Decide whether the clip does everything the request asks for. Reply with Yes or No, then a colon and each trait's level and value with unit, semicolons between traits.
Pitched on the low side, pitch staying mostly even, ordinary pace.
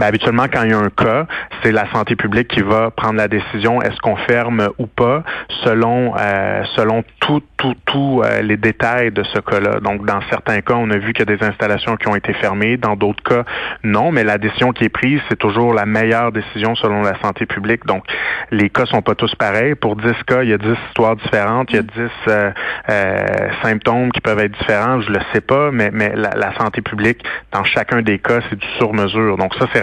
No: low, 110 Hz; narrow, 2.1 semitones; fast, 235 wpm